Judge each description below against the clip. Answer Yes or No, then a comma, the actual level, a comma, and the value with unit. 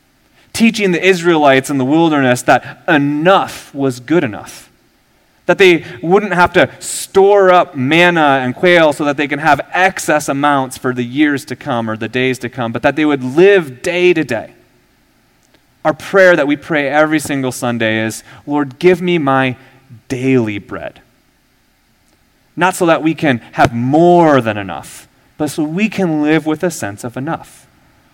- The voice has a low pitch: No, medium, 150 Hz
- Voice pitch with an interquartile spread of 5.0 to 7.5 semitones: Yes, wide, 5.4 semitones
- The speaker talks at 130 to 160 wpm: No, average, 170 wpm